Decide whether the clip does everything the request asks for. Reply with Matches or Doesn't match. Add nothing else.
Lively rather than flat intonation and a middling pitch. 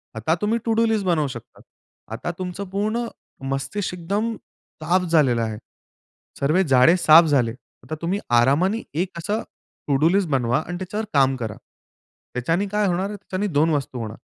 Matches